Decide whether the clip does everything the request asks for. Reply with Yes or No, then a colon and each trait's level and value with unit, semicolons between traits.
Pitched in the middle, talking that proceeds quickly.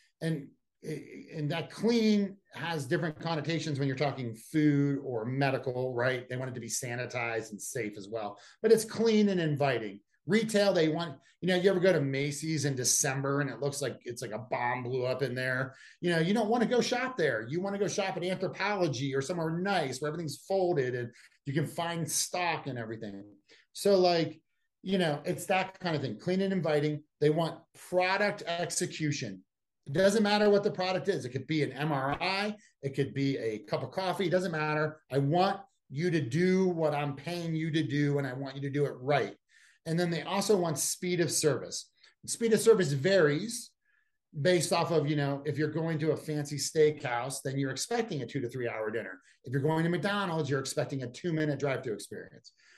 Yes: medium, 155 Hz; fast, 210 wpm